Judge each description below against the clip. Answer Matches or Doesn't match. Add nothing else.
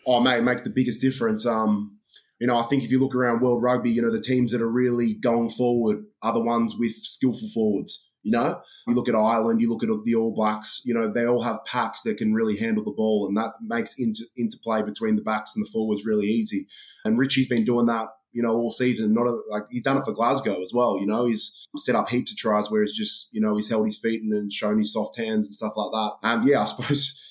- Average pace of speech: Doesn't match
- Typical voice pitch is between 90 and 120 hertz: Matches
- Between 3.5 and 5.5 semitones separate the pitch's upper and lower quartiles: Doesn't match